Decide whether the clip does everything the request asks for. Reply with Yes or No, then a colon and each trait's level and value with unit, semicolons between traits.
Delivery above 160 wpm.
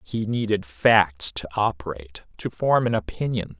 No: average, 150 wpm